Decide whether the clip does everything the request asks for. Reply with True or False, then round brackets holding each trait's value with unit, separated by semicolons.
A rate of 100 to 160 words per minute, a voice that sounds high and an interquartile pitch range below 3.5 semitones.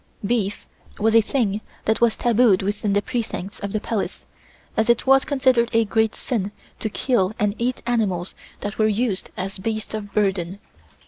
False (175 wpm; 215 Hz; 2.7 semitones)